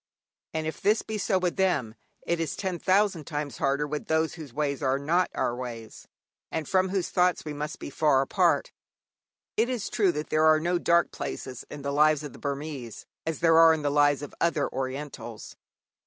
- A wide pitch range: No, average, 3.4 semitones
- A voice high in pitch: No, medium, 155 Hz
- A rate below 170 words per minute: No, average, 200 wpm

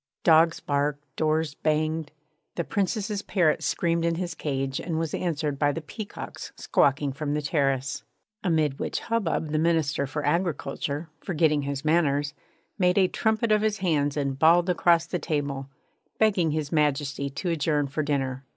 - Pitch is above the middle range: No, medium, 155 Hz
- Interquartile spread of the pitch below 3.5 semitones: Yes, average, 3.1 semitones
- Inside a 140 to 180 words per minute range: Yes, average, 160 wpm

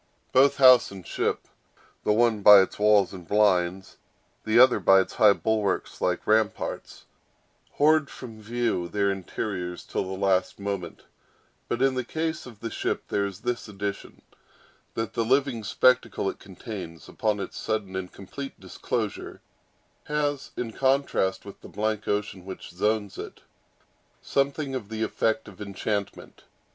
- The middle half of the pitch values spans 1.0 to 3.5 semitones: No, average, 3.9 semitones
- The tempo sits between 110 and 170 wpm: Yes, average, 145 wpm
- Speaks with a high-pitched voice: No, low, 105 Hz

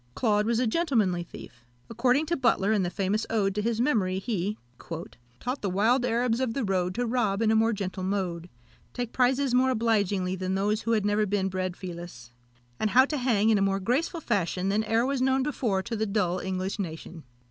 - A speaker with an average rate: No, fast, 210 wpm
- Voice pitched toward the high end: Yes, high, 210 Hz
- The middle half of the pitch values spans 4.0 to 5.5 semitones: Yes, average, 4.3 semitones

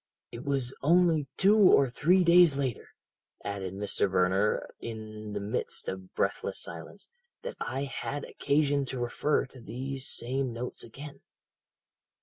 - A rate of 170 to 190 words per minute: No, slow, 135 wpm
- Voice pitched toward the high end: No, low, 130 Hz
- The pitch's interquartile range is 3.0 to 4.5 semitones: No, average, 5.1 semitones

